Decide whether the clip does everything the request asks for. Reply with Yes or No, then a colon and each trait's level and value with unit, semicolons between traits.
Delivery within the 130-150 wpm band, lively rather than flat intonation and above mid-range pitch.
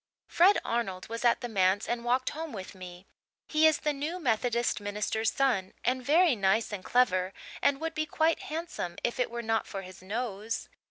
No: average, 195 wpm; wide, 6.1 semitones; high, 235 Hz